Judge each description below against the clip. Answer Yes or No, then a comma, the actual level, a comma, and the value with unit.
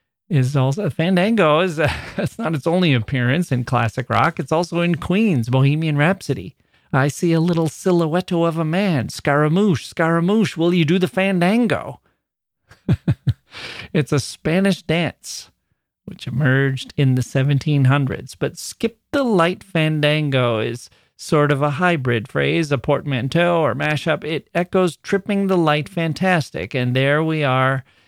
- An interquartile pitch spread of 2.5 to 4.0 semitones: No, average, 4.5 semitones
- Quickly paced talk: No, average, 145 wpm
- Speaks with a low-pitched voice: No, medium, 155 Hz